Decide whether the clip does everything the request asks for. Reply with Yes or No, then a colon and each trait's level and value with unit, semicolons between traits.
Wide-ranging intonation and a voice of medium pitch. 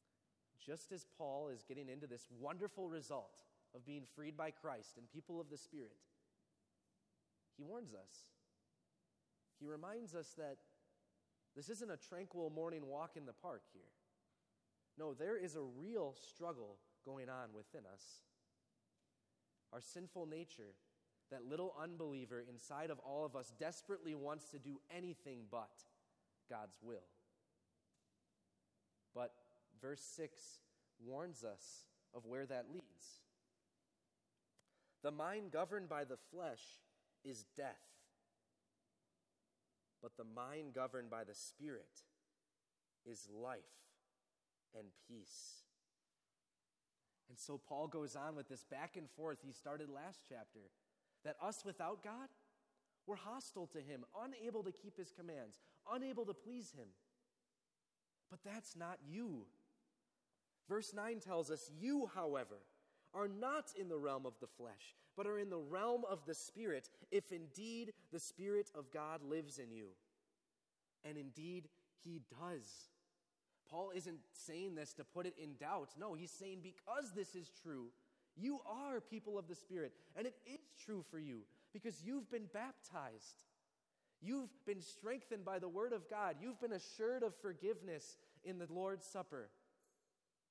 Yes: wide, 6.6 semitones; medium, 160 Hz